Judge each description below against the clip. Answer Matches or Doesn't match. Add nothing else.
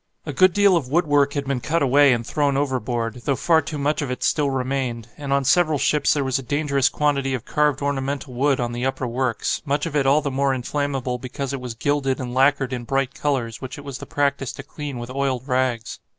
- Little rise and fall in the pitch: Matches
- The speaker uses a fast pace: Matches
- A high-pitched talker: Doesn't match